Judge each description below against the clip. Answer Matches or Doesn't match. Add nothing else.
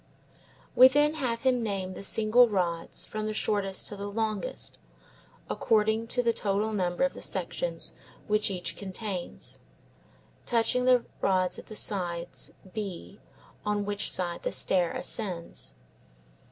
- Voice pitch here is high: Matches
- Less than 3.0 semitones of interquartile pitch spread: Doesn't match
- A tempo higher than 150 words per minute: Doesn't match